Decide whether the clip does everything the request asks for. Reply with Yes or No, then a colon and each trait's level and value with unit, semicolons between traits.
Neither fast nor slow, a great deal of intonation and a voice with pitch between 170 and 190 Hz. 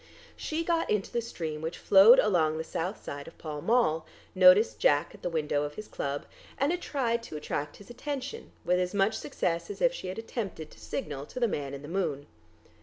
No: fast, 210 wpm; wide, 7.2 semitones; medium, 185 Hz